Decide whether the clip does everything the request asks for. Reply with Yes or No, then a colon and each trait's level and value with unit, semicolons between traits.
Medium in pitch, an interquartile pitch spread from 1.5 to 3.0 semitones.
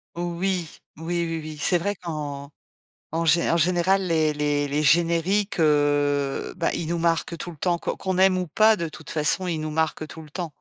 Yes: medium, 165 Hz; narrow, 2.5 semitones